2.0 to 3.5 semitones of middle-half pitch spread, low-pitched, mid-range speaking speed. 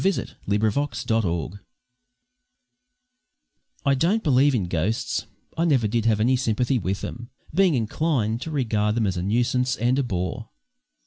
No: average, 4.0 semitones; low, 120 Hz; average, 165 wpm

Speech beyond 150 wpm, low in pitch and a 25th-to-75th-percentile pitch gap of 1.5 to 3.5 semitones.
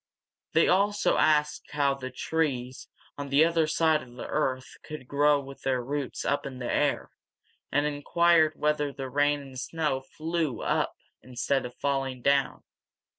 No: average, 160 wpm; medium, 145 Hz; narrow, 2.6 semitones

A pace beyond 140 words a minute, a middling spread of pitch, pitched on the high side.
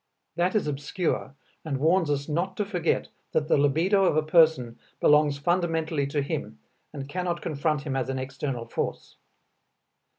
No: average, 160 wpm; average, 3.6 semitones; medium, 150 Hz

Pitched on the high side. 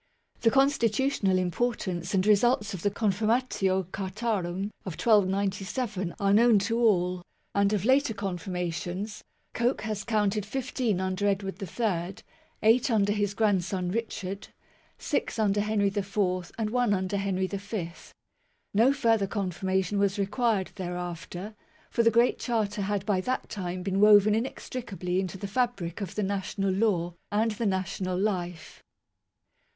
Yes: high, 200 Hz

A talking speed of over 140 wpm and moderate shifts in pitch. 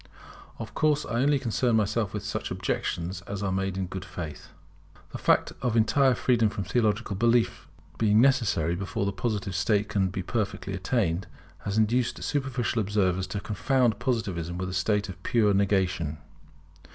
Yes: average, 165 wpm; average, 3.8 semitones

